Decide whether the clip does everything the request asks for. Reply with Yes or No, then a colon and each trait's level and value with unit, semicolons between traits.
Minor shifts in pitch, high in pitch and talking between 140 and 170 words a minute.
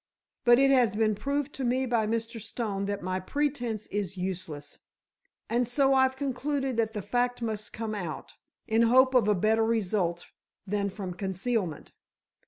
No: average, 3.8 semitones; high, 225 Hz; average, 165 wpm